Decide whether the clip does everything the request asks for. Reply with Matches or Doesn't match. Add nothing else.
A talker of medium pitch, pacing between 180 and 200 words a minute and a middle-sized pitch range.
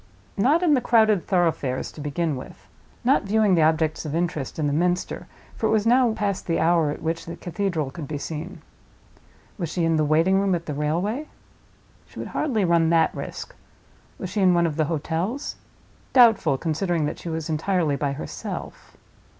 Matches